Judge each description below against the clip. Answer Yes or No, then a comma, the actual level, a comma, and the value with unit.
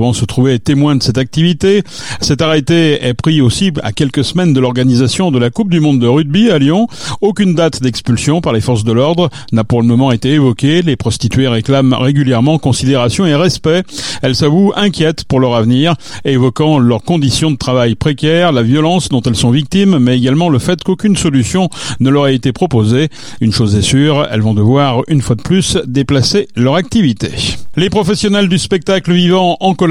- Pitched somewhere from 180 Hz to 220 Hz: No, medium, 140 Hz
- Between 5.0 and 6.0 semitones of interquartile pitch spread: Yes, wide, 5.4 semitones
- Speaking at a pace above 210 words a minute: No, average, 195 wpm